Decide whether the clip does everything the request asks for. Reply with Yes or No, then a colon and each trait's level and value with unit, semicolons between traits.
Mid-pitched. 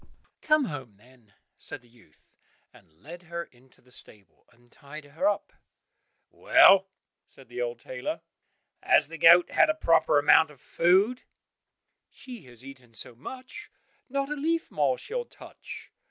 Yes: medium, 145 Hz